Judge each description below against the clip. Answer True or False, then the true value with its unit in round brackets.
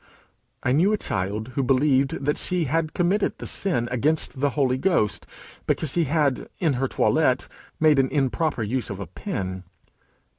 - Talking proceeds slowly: False (160 wpm)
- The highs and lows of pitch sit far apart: False (4.2 semitones)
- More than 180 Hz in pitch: False (135 Hz)